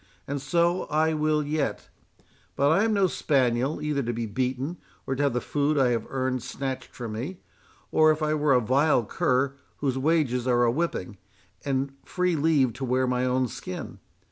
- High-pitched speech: No, low, 135 Hz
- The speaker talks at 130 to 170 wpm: No, average, 185 wpm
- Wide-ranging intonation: No, average, 3.5 semitones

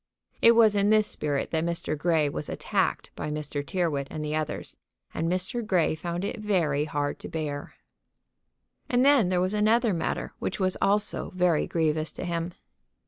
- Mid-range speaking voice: Yes, medium, 170 Hz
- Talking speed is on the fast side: No, average, 175 wpm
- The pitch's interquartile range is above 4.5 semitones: Yes, average, 4.9 semitones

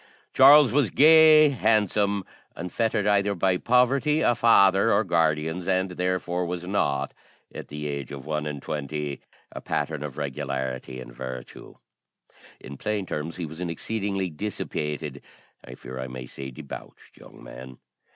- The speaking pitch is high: No, very low, 85 Hz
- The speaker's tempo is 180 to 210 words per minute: No, average, 150 wpm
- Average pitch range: No, wide, 6.4 semitones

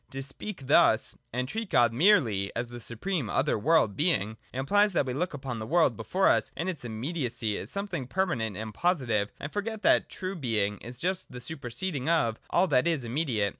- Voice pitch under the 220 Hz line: Yes, low, 135 Hz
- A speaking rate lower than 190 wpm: No, average, 195 wpm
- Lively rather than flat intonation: Yes, wide, 7.2 semitones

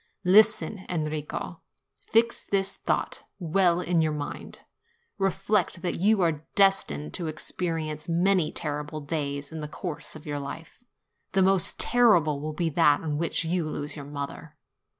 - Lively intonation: No, average, 4.0 semitones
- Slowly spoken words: No, average, 150 wpm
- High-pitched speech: No, medium, 165 Hz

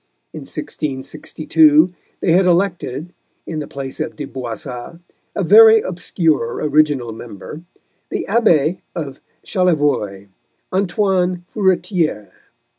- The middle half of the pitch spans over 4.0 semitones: Yes, average, 5.0 semitones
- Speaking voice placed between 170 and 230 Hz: No, medium, 160 Hz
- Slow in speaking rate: Yes, slow, 105 wpm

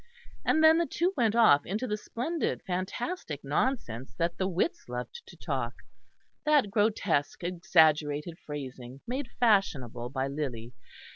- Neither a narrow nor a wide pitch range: No, wide, 8.9 semitones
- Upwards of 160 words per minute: No, slow, 135 wpm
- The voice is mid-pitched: Yes, medium, 175 Hz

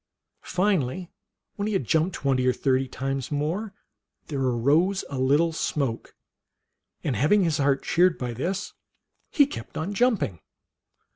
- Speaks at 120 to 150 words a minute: Yes, average, 145 wpm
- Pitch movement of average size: No, wide, 5.8 semitones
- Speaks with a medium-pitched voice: Yes, medium, 150 Hz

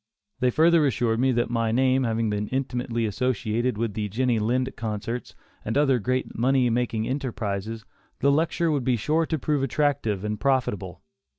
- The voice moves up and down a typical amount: Yes, average, 3.2 semitones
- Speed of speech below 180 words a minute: Yes, average, 170 wpm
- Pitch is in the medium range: No, low, 120 Hz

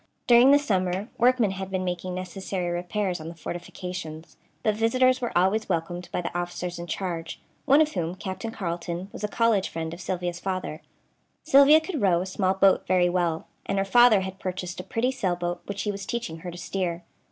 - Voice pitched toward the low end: No, medium, 185 Hz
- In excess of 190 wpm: Yes, average, 200 wpm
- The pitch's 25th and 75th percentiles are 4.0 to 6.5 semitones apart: No, average, 3.4 semitones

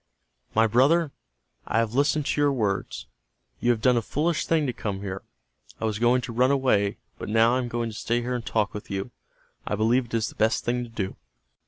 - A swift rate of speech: Yes, fast, 225 wpm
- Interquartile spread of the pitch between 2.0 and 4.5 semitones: Yes, average, 2.7 semitones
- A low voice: Yes, low, 120 Hz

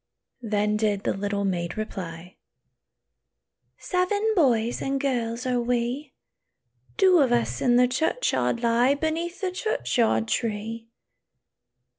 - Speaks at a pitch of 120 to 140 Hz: No, high, 240 Hz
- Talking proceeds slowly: Yes, slow, 115 wpm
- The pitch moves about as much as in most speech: Yes, average, 4.9 semitones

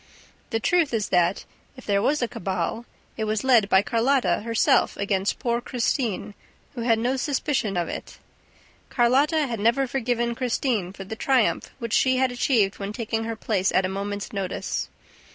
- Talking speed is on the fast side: No, average, 170 wpm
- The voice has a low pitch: No, high, 230 Hz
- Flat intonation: No, average, 4.0 semitones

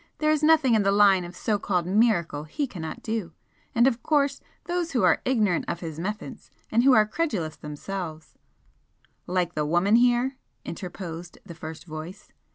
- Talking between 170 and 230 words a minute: Yes, average, 175 wpm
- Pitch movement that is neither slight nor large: No, wide, 6.1 semitones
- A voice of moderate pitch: No, high, 195 Hz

